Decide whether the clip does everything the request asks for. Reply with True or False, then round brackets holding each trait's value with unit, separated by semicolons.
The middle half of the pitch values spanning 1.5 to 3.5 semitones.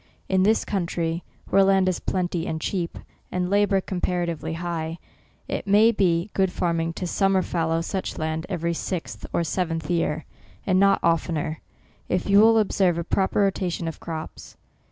True (2.7 semitones)